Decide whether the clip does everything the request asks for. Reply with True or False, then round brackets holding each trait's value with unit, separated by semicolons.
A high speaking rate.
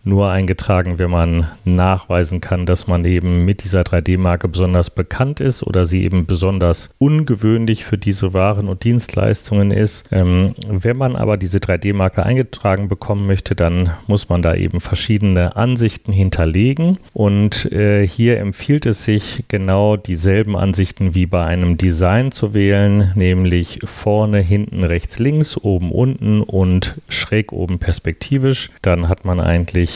False (145 wpm)